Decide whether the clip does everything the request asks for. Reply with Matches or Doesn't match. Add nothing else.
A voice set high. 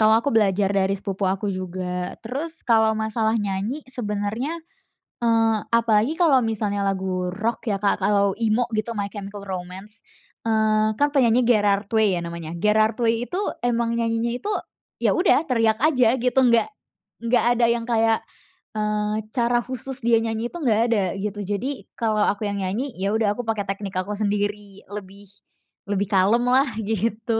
Matches